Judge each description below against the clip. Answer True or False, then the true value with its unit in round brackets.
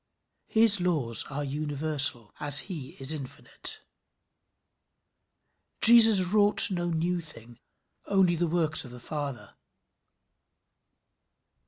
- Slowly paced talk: True (100 wpm)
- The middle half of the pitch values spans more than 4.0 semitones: True (4.5 semitones)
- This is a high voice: False (155 Hz)